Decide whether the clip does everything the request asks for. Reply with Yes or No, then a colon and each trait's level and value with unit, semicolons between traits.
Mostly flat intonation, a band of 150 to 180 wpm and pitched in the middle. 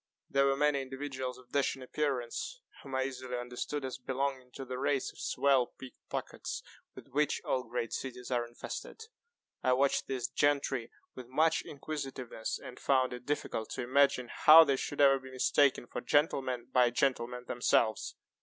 No: narrow, 2.1 semitones; average, 165 wpm; low, 130 Hz